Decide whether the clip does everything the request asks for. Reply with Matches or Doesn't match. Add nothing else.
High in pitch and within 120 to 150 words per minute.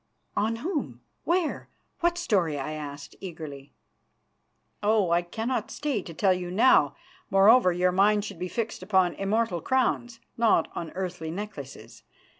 Matches